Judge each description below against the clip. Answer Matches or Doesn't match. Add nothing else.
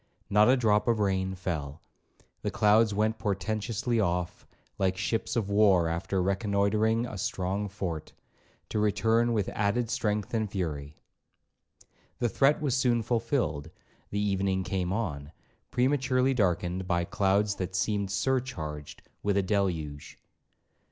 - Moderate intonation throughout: Matches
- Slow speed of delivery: Matches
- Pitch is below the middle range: Matches